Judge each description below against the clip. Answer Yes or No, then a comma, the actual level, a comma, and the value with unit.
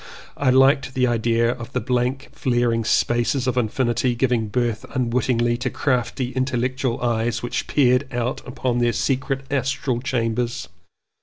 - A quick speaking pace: No, average, 145 wpm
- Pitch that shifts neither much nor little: No, narrow, 1.6 semitones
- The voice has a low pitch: Yes, low, 125 Hz